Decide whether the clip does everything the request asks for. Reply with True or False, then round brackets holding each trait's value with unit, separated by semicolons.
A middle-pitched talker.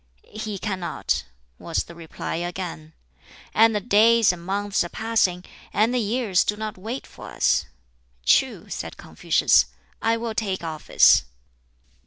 False (205 Hz)